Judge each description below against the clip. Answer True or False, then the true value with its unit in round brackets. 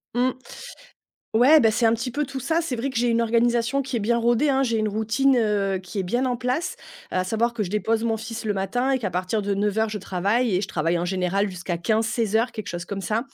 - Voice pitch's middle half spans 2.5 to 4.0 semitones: True (3.5 semitones)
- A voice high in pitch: True (225 Hz)